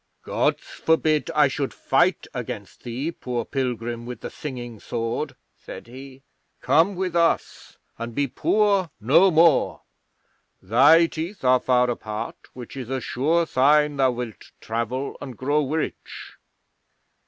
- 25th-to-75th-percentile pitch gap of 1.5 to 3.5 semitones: No, average, 4.5 semitones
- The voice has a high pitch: No, low, 135 Hz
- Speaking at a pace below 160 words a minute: Yes, slow, 135 wpm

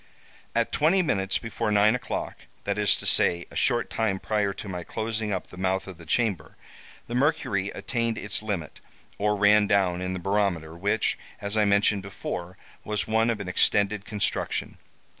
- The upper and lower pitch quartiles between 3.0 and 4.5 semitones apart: No, narrow, 2.5 semitones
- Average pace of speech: Yes, average, 175 wpm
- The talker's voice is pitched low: Yes, low, 100 Hz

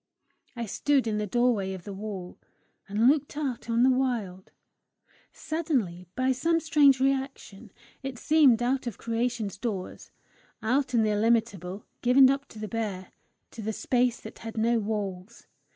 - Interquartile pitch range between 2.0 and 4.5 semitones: Yes, average, 4.0 semitones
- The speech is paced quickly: No, average, 155 wpm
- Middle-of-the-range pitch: No, high, 230 Hz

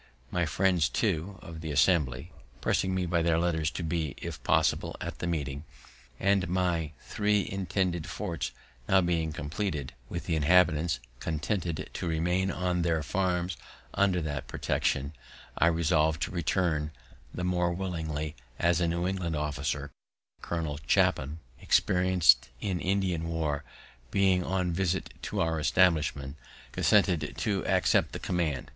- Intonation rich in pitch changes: No, average, 3.0 semitones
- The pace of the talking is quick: No, average, 140 wpm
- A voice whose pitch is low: Yes, very low, 85 Hz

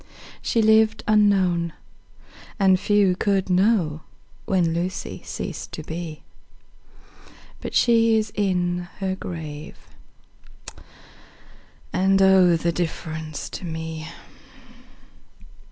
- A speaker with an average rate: No, slow, 95 wpm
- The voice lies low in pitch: No, medium, 185 Hz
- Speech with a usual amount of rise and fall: Yes, average, 3.4 semitones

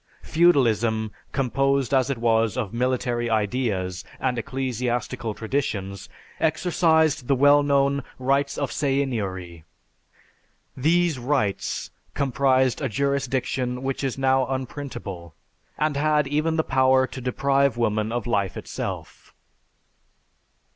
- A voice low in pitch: Yes, low, 130 Hz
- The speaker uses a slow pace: Yes, slow, 110 wpm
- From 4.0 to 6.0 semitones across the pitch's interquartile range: No, average, 3.2 semitones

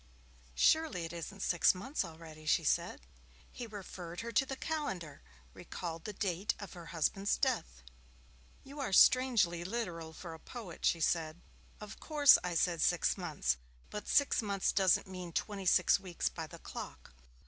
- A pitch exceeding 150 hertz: Yes, medium, 185 Hz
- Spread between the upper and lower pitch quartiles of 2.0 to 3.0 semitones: No, average, 4.6 semitones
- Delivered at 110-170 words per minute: Yes, average, 160 wpm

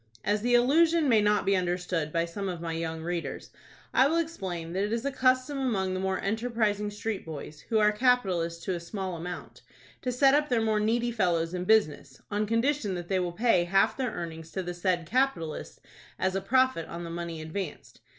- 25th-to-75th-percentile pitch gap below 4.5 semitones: No, wide, 5.5 semitones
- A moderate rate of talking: No, fast, 210 wpm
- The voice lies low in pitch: No, high, 195 Hz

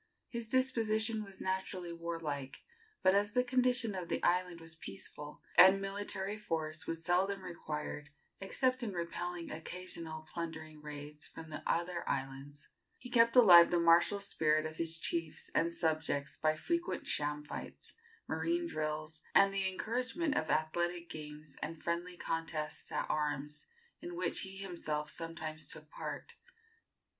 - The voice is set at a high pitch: No, medium, 170 Hz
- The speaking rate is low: No, average, 145 wpm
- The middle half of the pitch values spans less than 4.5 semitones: Yes, average, 4.1 semitones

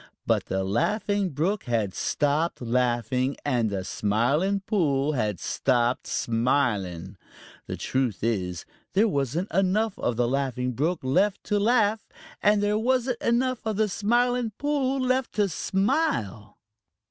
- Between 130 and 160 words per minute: Yes, slow, 135 wpm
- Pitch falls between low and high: Yes, medium, 155 Hz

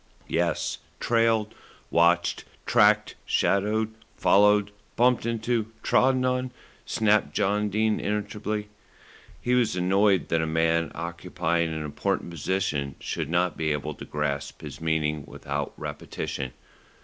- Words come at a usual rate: No, slow, 120 wpm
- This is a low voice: Yes, very low, 95 Hz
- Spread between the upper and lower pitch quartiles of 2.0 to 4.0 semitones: No, average, 5.0 semitones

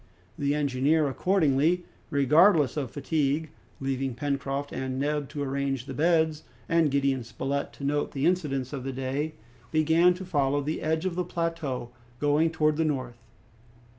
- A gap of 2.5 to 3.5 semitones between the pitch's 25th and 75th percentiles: Yes, average, 2.8 semitones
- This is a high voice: No, medium, 145 Hz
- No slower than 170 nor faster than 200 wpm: No, average, 155 wpm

